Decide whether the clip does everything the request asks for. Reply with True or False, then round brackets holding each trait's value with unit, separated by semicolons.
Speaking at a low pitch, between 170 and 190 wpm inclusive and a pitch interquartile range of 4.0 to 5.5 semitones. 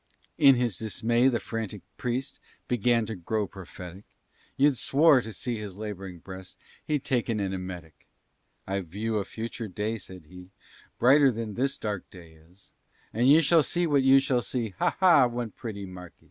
True (110 Hz; 175 wpm; 4.8 semitones)